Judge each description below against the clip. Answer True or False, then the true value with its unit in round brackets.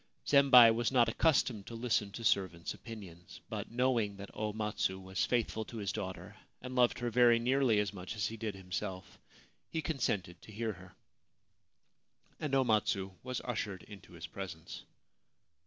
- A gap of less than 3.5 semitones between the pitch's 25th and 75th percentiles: False (4.1 semitones)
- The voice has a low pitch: True (110 Hz)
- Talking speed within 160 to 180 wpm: True (165 wpm)